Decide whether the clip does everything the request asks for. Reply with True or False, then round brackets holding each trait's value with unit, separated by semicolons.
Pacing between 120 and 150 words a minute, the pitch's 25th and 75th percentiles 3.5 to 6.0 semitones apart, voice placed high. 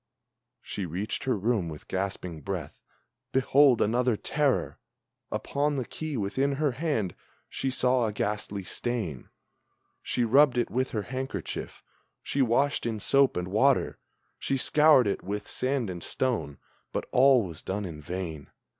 False (145 wpm; 5.4 semitones; 120 Hz)